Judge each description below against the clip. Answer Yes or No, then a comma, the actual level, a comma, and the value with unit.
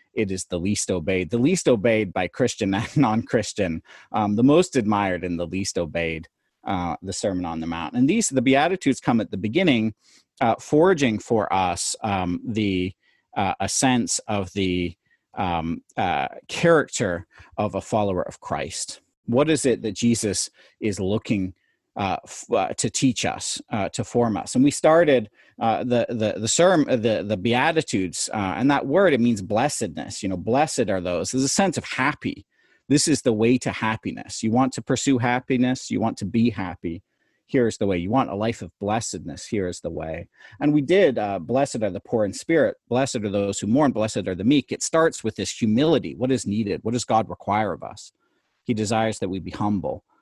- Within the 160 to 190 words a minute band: No, average, 200 wpm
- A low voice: Yes, low, 110 Hz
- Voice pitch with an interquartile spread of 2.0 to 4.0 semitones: No, average, 4.7 semitones